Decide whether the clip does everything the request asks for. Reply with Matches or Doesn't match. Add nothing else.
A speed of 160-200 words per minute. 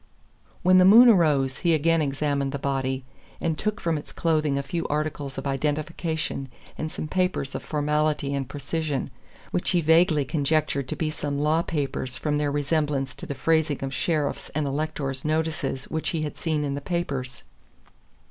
Matches